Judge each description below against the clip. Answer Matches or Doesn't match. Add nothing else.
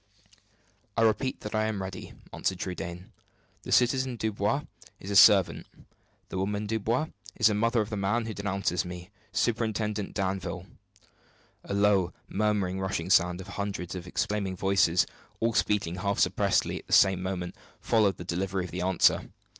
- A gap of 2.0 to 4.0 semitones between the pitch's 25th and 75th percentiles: Matches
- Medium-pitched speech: Doesn't match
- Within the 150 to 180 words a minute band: Matches